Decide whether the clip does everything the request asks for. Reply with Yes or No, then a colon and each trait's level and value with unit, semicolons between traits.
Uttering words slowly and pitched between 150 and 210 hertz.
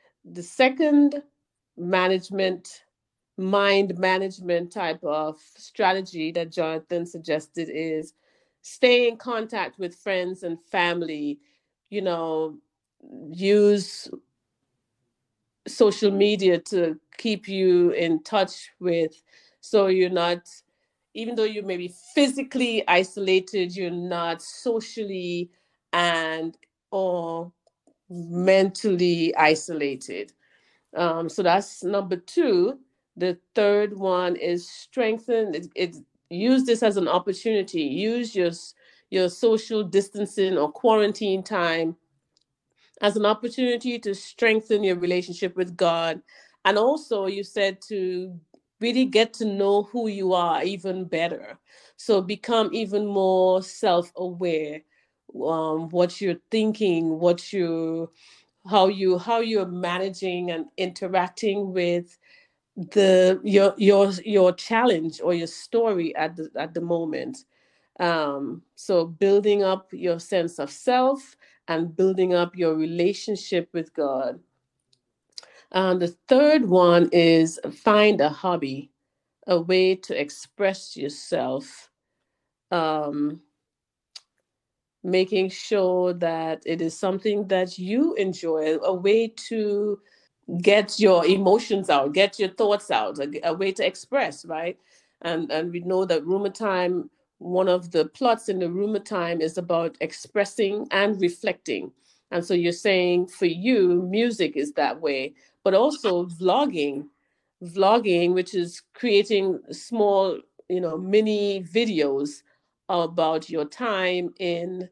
Yes: slow, 120 wpm; medium, 185 Hz